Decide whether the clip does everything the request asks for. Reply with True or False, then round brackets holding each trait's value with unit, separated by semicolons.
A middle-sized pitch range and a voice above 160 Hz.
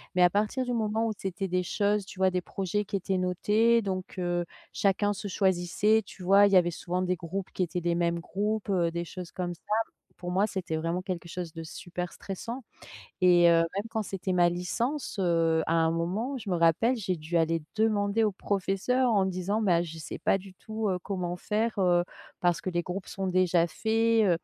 True (3.0 semitones; 185 Hz)